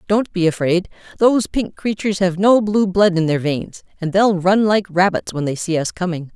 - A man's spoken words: No, female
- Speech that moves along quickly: Yes, fast, 215 wpm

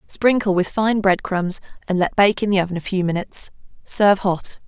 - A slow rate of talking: No, fast, 205 wpm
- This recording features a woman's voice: Yes, female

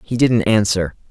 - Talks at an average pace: Yes, average, 160 wpm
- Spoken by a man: Yes, male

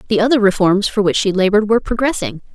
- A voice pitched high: Yes, high, 205 Hz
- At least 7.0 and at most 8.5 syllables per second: Yes, 7.1 syllables/s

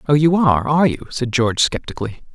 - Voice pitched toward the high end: No, low, 135 Hz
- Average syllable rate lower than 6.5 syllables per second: No, 6.8 syllables/s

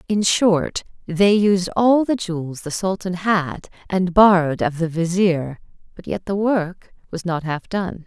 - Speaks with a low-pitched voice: No, medium, 185 Hz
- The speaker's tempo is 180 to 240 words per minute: No, average, 170 wpm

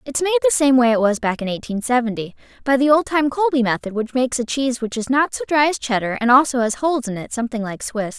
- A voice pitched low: No, very high, 255 Hz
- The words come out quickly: Yes, fast, 270 wpm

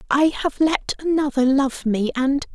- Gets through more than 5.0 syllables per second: No, 4.2 syllables/s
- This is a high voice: Yes, very high, 280 Hz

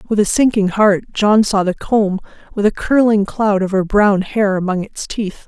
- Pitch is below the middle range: No, high, 205 Hz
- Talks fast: Yes, fast, 210 wpm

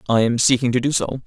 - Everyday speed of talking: No, fast, 285 wpm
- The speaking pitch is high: No, low, 125 Hz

